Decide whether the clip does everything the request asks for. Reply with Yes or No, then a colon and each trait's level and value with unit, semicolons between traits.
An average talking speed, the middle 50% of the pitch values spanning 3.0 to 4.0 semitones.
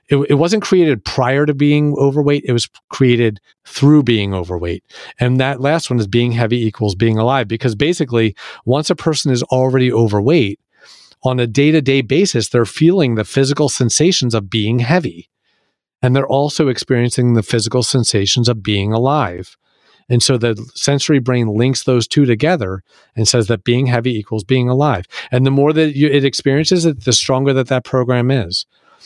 Yes: average, 175 wpm; average, 3.4 semitones